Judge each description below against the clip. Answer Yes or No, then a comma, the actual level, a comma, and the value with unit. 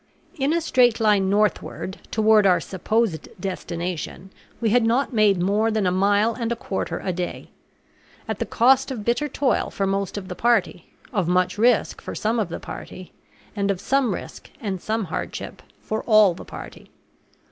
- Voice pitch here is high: Yes, high, 210 Hz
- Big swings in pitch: No, average, 3.7 semitones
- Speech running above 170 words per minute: Yes, average, 180 wpm